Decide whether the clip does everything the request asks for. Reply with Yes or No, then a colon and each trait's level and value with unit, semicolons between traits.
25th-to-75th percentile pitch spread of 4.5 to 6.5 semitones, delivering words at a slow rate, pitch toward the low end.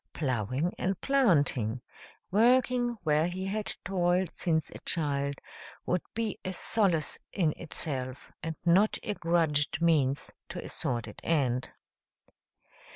No: average, 5.1 semitones; slow, 120 wpm; medium, 165 Hz